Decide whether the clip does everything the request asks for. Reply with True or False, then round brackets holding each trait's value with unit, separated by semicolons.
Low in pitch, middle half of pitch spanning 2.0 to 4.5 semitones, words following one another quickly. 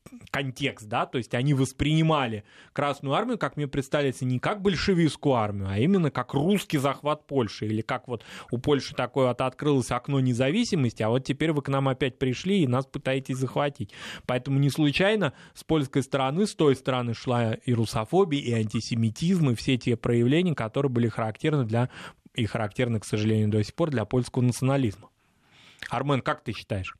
True (130 Hz; 3.4 semitones; 175 wpm)